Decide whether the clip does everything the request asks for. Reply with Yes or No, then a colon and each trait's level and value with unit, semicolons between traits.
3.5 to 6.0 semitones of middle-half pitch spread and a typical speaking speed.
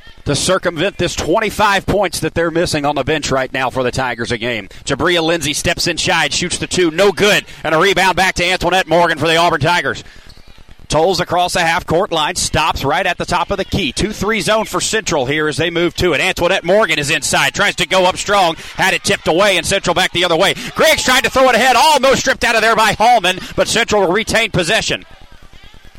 No: average, 4.0 semitones; fast, 230 wpm